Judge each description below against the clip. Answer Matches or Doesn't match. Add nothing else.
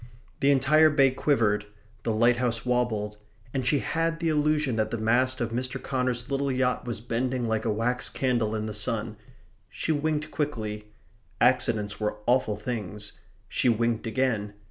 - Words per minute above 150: Matches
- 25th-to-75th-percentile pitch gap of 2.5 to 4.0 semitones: Matches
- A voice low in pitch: Matches